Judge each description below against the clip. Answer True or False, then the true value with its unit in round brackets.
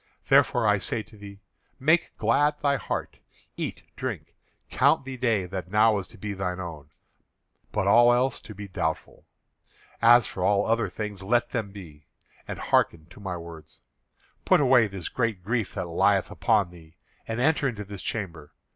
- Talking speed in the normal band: True (175 wpm)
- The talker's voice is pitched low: True (105 Hz)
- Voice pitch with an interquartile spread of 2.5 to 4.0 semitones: False (4.4 semitones)